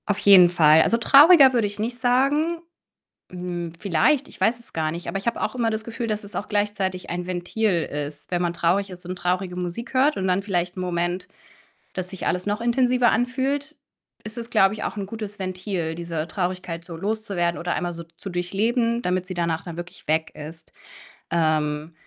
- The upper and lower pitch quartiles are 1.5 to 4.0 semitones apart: No, average, 4.6 semitones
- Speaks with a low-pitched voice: No, medium, 185 Hz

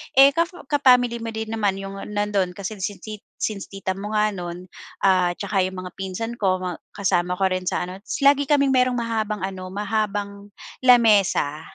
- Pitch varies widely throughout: No, average, 3.3 semitones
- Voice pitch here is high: Yes, high, 205 Hz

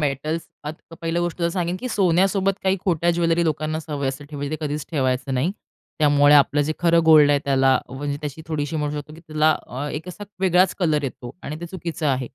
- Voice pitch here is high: No, medium, 155 Hz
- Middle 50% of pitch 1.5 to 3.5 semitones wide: Yes, average, 2.9 semitones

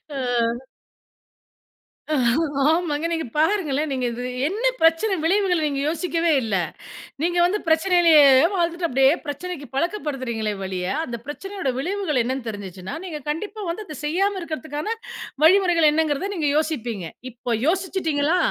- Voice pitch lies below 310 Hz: No, very high, 320 Hz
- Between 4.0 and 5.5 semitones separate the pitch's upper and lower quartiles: Yes, average, 4.7 semitones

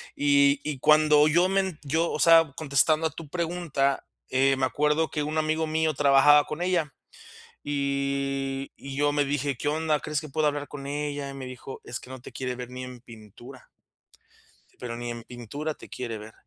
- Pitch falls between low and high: Yes, medium, 145 Hz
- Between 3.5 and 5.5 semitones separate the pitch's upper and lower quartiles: No, narrow, 2.4 semitones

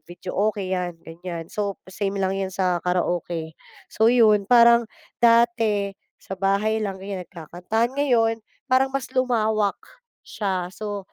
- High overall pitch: Yes, high, 200 Hz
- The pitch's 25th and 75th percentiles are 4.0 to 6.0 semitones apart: No, average, 3.5 semitones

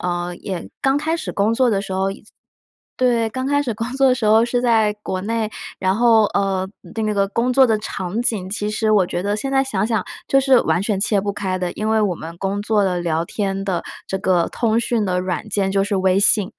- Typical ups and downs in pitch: Yes, average, 3.3 semitones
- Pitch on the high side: Yes, high, 210 Hz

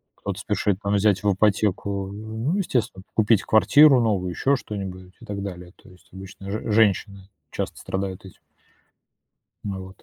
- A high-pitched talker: No, low, 100 Hz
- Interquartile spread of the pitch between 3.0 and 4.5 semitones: No, narrow, 2.4 semitones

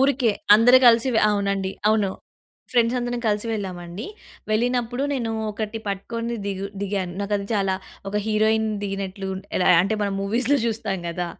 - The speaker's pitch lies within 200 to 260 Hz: Yes, high, 210 Hz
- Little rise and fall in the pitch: No, average, 3.0 semitones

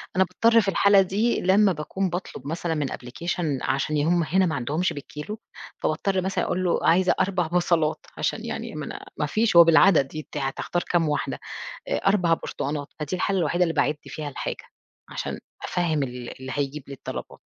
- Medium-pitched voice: Yes, medium, 170 Hz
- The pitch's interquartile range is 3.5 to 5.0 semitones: Yes, average, 4.0 semitones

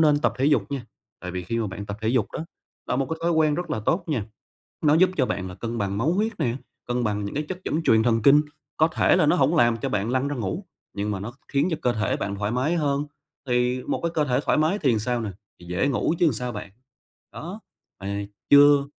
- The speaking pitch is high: No, low, 125 Hz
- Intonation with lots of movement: Yes, wide, 6.0 semitones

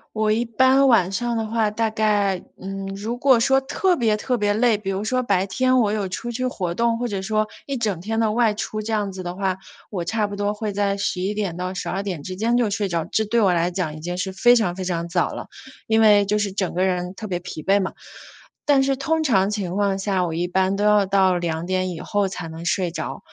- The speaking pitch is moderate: No, high, 205 Hz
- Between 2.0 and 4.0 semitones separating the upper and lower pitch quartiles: Yes, average, 3.3 semitones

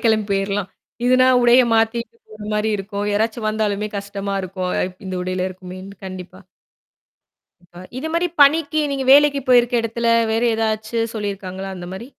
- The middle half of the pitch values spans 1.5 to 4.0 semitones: Yes, average, 3.7 semitones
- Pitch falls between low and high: No, high, 210 Hz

